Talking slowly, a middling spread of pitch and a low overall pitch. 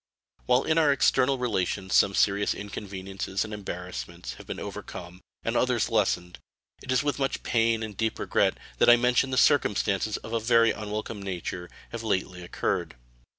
No: average, 160 wpm; average, 4.1 semitones; low, 110 Hz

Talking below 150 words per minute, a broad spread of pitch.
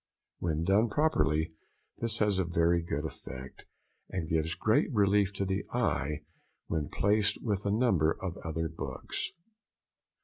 No: average, 140 wpm; average, 4.4 semitones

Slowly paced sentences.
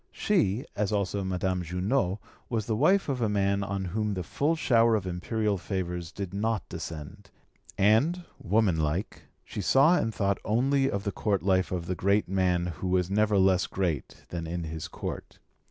No: average, 175 wpm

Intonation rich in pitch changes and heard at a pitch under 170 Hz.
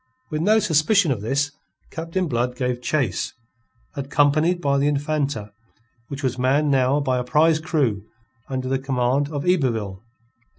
No: average, 3.4 semitones; medium, 140 Hz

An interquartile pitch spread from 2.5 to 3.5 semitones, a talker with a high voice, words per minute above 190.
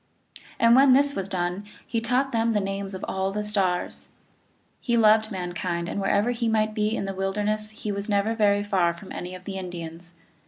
Yes: average, 2.8 semitones; high, 205 Hz; average, 200 wpm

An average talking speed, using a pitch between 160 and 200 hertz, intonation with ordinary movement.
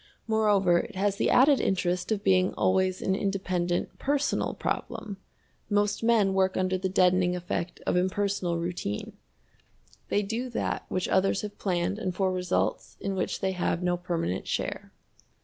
No: average, 155 wpm; high, 190 Hz; narrow, 2.2 semitones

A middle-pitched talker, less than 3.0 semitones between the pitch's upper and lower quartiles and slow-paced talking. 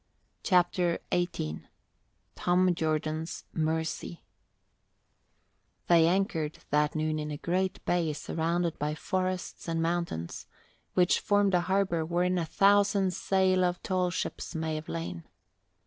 Yes: medium, 175 Hz; narrow, 2.6 semitones; slow, 120 wpm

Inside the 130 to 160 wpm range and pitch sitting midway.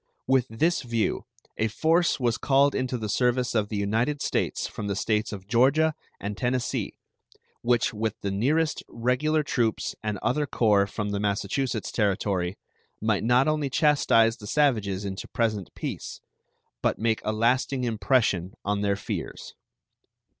No: average, 150 wpm; low, 115 Hz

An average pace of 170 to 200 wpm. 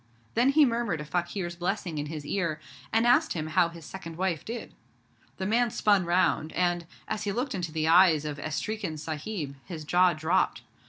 Yes: average, 190 wpm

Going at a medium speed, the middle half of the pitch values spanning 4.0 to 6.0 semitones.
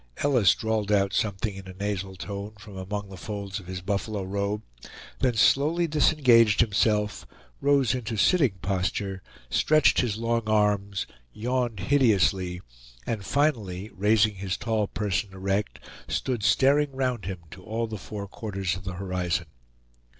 No: average, 145 wpm; average, 3.1 semitones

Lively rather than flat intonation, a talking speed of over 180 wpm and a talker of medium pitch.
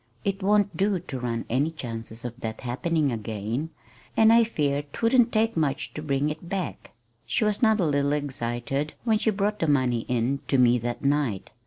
Yes: wide, 8.2 semitones; average, 190 wpm; medium, 145 Hz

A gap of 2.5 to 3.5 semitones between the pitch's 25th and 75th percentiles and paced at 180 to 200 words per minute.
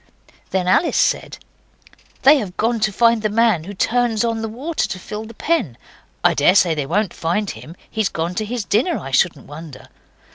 No: average, 4.9 semitones; average, 190 wpm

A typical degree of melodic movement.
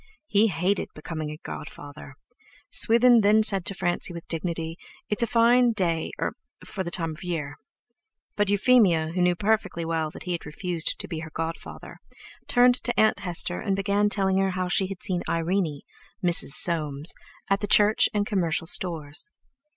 Yes: average, 3.9 semitones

